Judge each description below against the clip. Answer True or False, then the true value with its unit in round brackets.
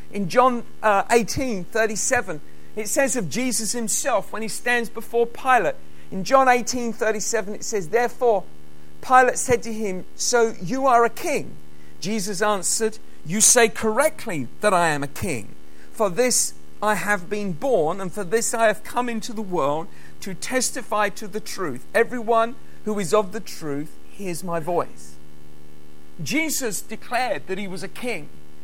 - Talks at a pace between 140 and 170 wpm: True (155 wpm)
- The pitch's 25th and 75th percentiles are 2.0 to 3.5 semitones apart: False (5.5 semitones)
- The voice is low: False (215 Hz)